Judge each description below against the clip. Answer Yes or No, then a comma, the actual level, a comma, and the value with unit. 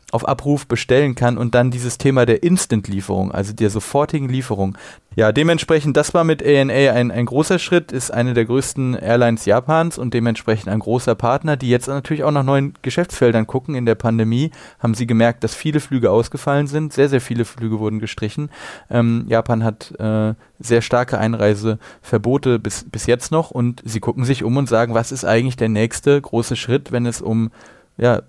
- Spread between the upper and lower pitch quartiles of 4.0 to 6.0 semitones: No, average, 3.6 semitones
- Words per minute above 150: Yes, fast, 190 wpm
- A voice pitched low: Yes, low, 120 Hz